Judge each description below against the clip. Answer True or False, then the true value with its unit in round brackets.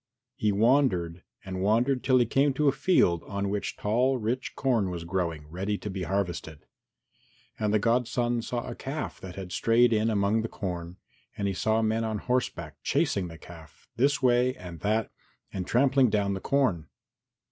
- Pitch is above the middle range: False (105 Hz)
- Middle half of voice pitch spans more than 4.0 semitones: True (4.9 semitones)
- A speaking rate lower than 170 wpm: False (180 wpm)